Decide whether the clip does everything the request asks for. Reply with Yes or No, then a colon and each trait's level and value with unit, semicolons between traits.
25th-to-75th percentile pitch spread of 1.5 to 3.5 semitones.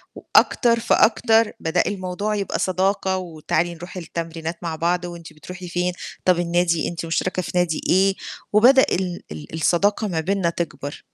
Yes: narrow, 2.4 semitones